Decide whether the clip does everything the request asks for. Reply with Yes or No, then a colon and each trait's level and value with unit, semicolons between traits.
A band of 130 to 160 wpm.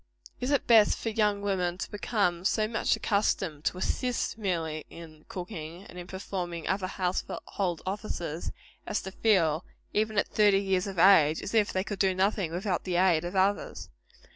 No: average, 175 wpm